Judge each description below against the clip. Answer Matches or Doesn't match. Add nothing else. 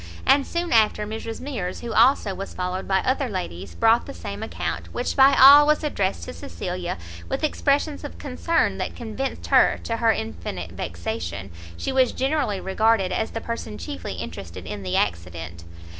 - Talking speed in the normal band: Matches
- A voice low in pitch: Doesn't match